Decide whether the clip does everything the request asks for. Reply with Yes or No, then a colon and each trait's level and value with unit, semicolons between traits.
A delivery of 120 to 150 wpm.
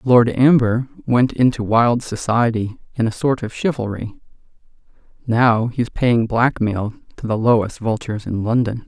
Yes: average, 140 wpm